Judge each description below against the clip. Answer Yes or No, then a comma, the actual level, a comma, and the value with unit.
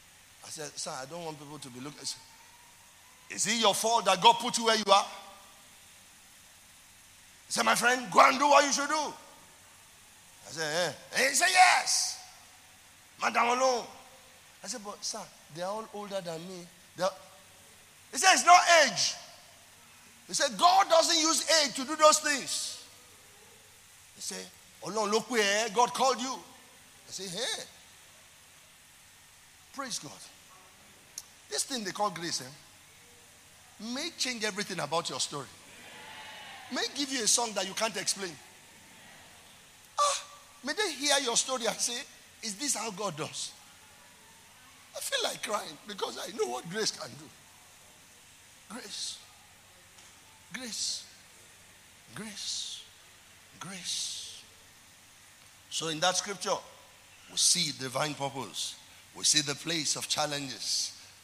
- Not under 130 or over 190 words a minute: Yes, average, 140 wpm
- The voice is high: Yes, high, 195 Hz